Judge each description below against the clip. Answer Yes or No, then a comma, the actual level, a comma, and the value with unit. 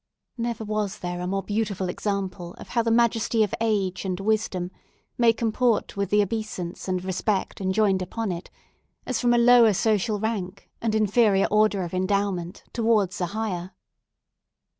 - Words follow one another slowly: No, average, 160 wpm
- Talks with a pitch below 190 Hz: No, high, 205 Hz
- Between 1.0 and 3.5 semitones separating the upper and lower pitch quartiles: Yes, average, 3.0 semitones